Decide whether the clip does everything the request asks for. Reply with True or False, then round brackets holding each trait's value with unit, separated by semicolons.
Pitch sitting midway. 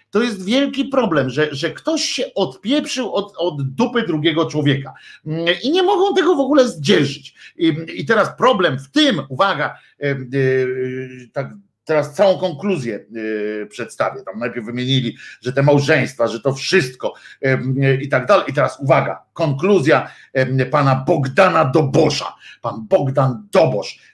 True (155 Hz)